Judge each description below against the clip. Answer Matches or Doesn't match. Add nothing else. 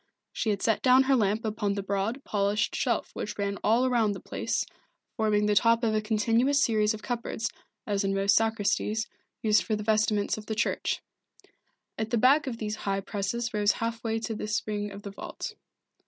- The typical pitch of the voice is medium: Doesn't match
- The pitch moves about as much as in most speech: Doesn't match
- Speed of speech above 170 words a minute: Matches